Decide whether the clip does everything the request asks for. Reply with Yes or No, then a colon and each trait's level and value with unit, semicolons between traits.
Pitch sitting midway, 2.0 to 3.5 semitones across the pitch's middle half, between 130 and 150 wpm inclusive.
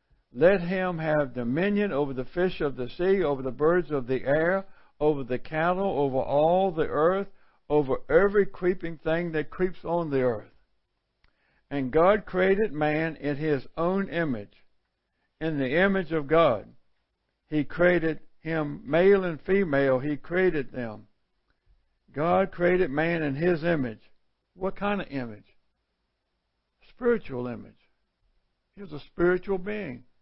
No: medium, 160 Hz; average, 5.0 semitones; average, 140 wpm